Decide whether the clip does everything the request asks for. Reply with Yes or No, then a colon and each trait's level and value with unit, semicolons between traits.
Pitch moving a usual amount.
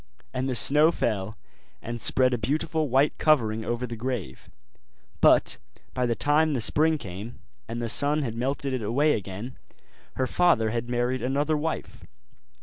Yes: average, 4.2 semitones